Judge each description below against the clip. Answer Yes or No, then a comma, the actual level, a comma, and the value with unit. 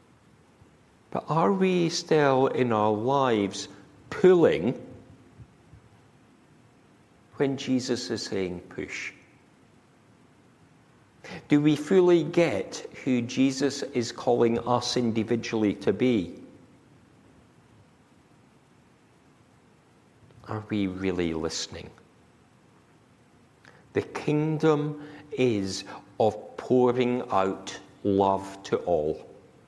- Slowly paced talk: Yes, slow, 75 wpm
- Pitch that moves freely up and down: Yes, wide, 6.5 semitones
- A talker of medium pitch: No, low, 125 Hz